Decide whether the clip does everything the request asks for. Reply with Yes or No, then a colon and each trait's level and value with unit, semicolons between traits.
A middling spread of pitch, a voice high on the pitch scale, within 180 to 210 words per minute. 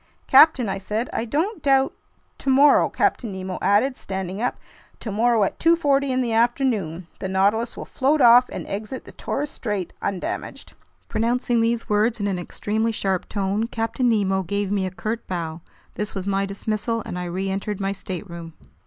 No: average, 4.0 semitones; high, 215 Hz; average, 170 wpm